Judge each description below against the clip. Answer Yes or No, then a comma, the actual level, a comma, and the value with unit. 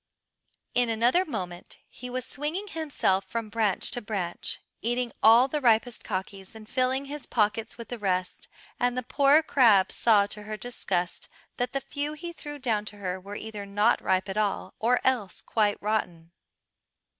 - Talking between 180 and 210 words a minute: No, average, 170 wpm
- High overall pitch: Yes, high, 225 Hz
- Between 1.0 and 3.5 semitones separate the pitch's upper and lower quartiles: No, average, 4.0 semitones